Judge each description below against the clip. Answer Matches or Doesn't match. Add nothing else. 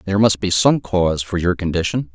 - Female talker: Doesn't match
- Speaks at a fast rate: Matches